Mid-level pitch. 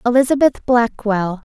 No: high, 235 Hz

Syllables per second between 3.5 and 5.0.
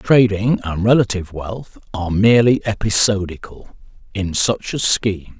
Yes: 4.7 syllables/s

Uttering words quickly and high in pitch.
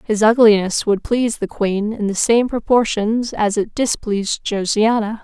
No: average, 160 wpm; high, 215 Hz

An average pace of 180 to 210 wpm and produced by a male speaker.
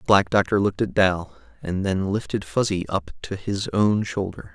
Yes: average, 200 wpm; male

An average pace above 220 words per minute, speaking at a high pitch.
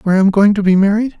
Yes: fast, 350 wpm; high, 200 Hz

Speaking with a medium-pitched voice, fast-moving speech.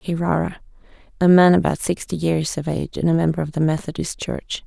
No: medium, 165 Hz; average, 195 wpm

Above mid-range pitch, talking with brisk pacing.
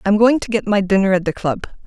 Yes: high, 200 Hz; fast, 290 wpm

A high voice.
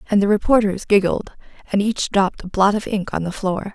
Yes: high, 200 Hz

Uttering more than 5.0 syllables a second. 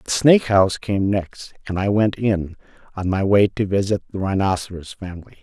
Yes: 5.3 syllables/s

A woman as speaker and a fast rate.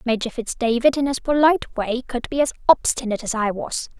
Yes: female; fast, 210 wpm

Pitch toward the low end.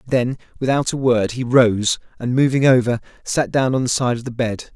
Yes: low, 125 Hz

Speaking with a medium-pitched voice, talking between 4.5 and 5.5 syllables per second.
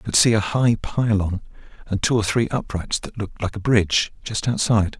No: low, 105 Hz; 5.4 syllables/s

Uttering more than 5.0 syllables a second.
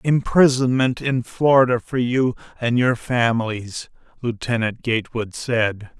No: 4.1 syllables/s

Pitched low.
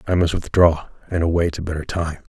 Yes: very low, 80 Hz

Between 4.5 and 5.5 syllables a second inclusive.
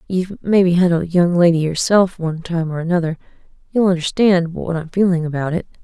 No: 5.8 syllables/s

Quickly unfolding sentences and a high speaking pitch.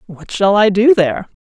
Yes: fast, 210 wpm; high, 205 Hz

